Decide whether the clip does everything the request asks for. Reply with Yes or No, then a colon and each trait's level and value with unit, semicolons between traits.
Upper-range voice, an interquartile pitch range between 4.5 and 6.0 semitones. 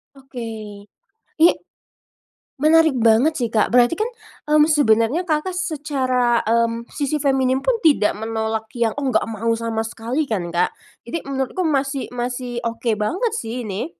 Yes: high, 245 Hz; average, 4.8 semitones